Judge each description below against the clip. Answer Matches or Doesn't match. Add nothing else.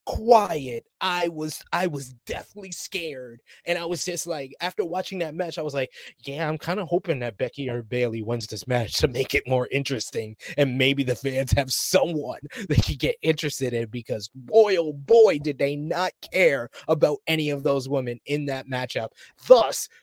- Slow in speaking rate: Doesn't match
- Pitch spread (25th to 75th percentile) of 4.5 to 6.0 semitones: Matches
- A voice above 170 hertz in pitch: Doesn't match